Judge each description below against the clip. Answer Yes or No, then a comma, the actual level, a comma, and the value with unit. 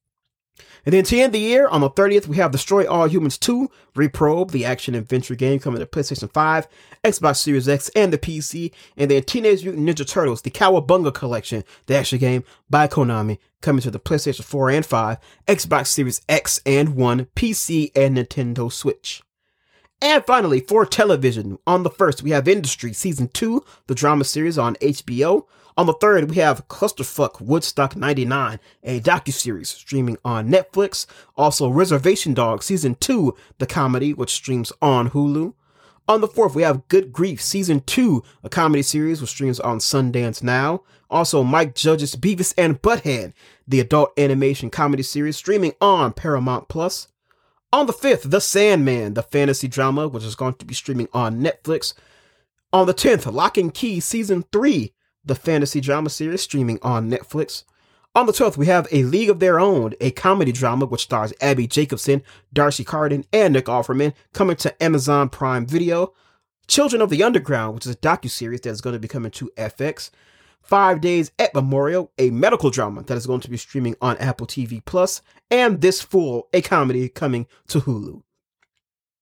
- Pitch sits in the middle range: Yes, medium, 145 Hz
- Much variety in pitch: Yes, wide, 5.9 semitones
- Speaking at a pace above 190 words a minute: No, average, 175 wpm